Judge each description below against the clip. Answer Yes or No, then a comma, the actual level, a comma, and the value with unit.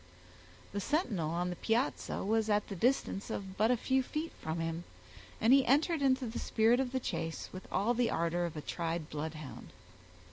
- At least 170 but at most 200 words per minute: Yes, average, 190 wpm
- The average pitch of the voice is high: Yes, high, 210 Hz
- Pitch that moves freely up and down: Yes, wide, 6.9 semitones